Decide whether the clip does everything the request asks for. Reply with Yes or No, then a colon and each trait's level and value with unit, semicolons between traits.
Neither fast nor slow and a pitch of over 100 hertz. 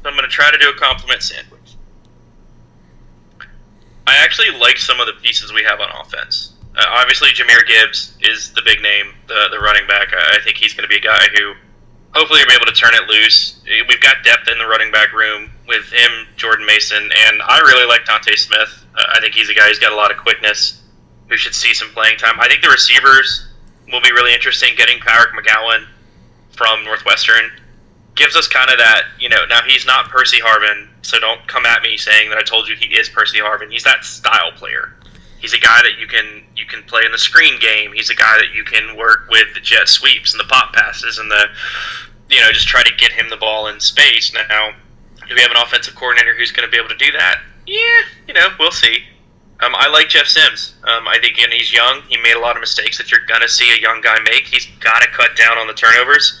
No: fast, 240 wpm; low, 110 Hz